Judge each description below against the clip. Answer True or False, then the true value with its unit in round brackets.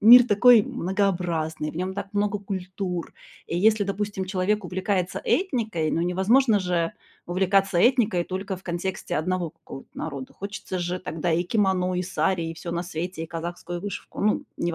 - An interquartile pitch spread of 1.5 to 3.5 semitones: True (2.8 semitones)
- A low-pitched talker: False (185 Hz)